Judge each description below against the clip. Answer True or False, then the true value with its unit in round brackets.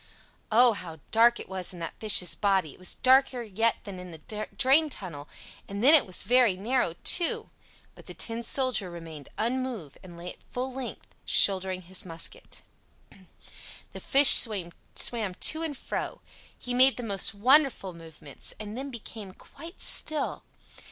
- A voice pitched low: False (215 Hz)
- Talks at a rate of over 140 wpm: True (160 wpm)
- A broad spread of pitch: True (5.8 semitones)